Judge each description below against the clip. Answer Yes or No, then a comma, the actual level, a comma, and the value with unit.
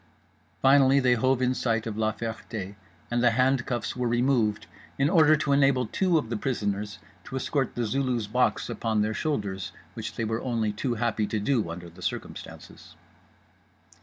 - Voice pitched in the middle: No, low, 120 Hz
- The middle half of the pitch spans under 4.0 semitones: Yes, average, 3.6 semitones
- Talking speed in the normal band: Yes, average, 170 wpm